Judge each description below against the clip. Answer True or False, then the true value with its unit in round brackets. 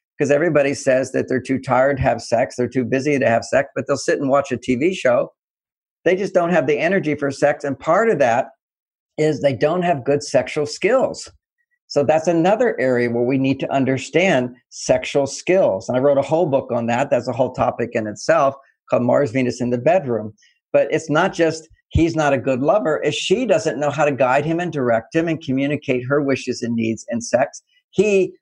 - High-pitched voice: False (140 Hz)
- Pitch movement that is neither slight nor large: True (3.7 semitones)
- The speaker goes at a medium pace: False (215 wpm)